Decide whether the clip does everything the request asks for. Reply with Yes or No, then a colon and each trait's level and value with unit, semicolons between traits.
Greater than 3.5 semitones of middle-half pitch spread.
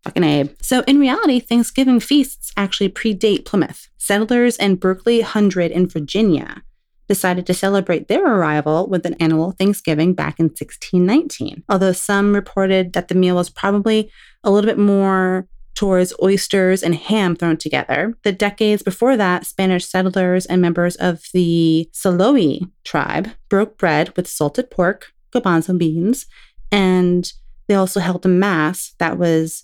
No: narrow, 2.6 semitones